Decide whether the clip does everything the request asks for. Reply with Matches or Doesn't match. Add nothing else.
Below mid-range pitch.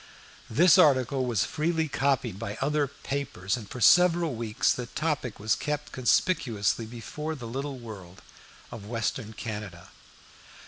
Matches